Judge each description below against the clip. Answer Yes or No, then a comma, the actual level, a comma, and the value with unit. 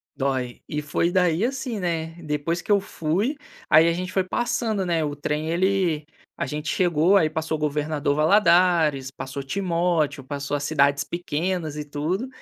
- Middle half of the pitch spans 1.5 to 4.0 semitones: Yes, average, 3.6 semitones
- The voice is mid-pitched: Yes, medium, 160 Hz